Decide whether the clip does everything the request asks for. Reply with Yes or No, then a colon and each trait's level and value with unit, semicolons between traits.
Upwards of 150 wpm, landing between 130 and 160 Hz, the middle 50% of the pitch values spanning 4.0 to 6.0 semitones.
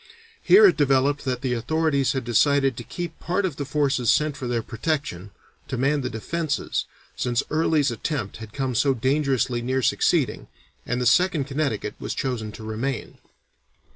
No: average, 170 wpm; low, 135 Hz; average, 3.5 semitones